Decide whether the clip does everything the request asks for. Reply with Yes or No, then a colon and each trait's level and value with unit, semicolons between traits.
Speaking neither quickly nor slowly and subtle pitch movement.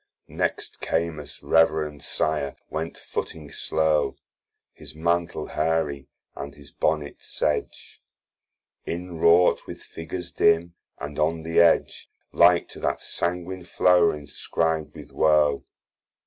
No: slow, 110 wpm; narrow, 2.2 semitones